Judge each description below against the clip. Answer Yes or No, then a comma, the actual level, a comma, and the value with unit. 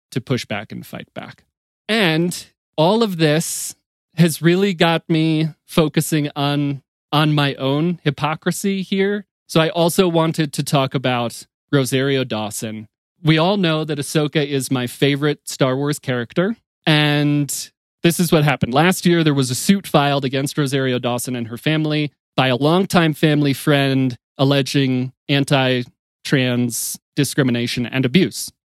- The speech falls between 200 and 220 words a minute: No, average, 145 wpm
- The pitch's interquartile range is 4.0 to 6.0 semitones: No, average, 3.5 semitones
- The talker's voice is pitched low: No, medium, 150 Hz